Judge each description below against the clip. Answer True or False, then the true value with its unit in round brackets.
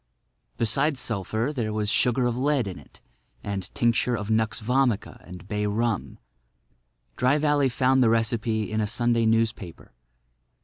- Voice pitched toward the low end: True (115 Hz)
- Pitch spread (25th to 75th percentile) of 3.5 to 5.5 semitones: False (2.9 semitones)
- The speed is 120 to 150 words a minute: True (145 wpm)